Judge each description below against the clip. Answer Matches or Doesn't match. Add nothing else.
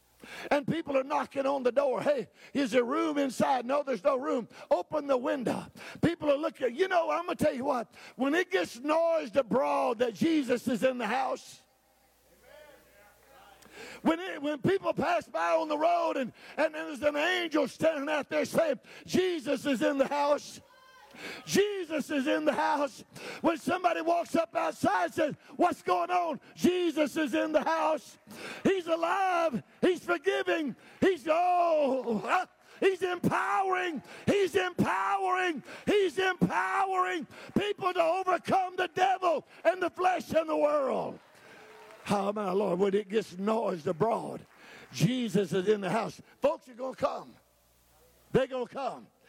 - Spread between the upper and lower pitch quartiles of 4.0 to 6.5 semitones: Matches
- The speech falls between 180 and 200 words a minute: Doesn't match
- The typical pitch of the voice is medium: Doesn't match